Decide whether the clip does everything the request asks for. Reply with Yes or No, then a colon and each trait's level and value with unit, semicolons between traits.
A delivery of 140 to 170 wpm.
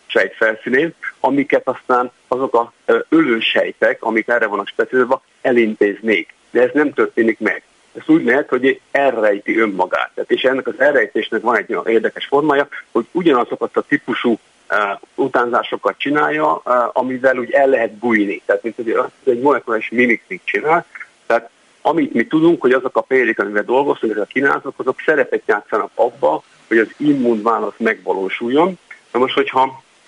Yes: fast, 155 wpm